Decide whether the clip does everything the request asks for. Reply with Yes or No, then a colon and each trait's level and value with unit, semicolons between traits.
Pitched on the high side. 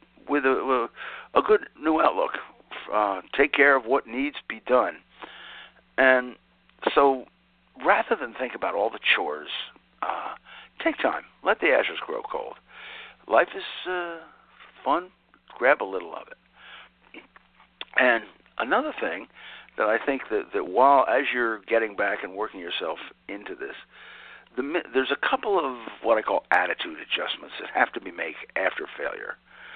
Yes: very high, 320 Hz